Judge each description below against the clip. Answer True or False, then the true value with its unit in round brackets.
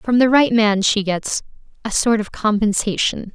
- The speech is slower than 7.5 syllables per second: True (4.5 syllables/s)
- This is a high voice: True (215 Hz)